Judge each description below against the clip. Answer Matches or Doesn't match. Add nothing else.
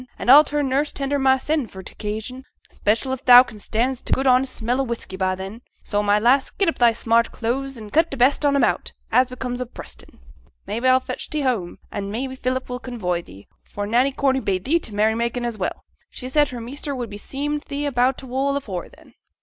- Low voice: Doesn't match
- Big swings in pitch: Doesn't match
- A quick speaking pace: Matches